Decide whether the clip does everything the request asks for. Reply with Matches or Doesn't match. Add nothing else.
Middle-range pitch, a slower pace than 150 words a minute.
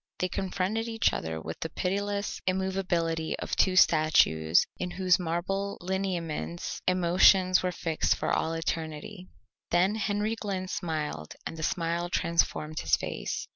Matches